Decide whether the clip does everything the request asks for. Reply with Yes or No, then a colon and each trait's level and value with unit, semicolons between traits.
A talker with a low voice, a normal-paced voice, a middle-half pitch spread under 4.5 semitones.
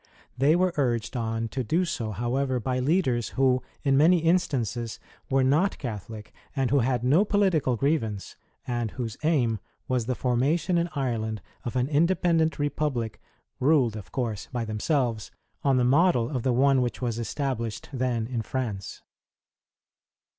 Yes: low, 130 Hz; average, 155 wpm; average, 3.9 semitones